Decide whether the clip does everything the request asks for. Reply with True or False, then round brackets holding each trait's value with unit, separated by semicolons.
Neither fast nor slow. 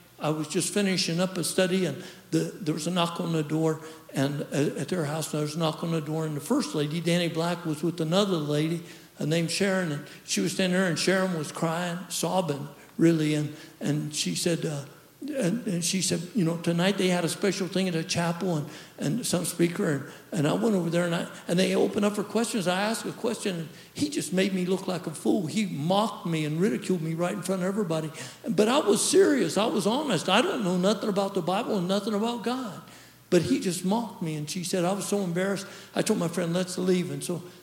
False (240 wpm)